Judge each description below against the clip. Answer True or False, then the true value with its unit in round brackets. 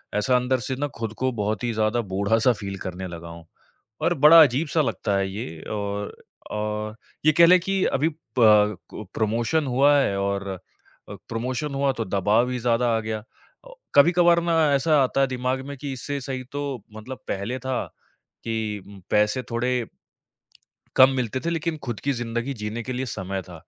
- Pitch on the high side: False (120 Hz)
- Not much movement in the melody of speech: False (4.5 semitones)